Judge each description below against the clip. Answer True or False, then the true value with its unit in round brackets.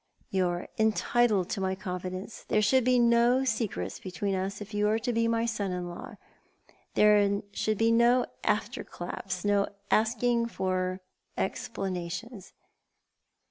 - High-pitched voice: True (210 Hz)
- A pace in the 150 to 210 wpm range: False (140 wpm)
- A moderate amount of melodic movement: True (3.7 semitones)